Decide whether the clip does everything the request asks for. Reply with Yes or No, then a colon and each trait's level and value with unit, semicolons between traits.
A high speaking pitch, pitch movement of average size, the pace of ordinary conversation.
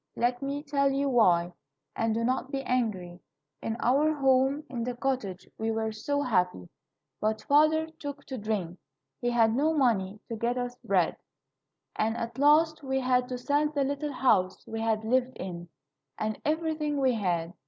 Yes: very high, 250 Hz; average, 4.4 semitones; average, 175 wpm